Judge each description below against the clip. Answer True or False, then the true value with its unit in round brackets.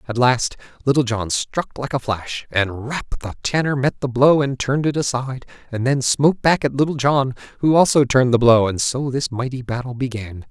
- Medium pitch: False (130 Hz)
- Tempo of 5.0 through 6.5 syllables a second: True (5.3 syllables/s)